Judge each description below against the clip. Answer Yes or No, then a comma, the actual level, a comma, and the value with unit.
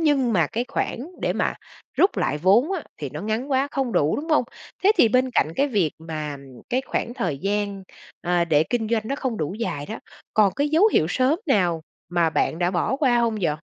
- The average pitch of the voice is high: Yes, high, 220 Hz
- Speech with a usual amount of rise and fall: No, wide, 7.5 semitones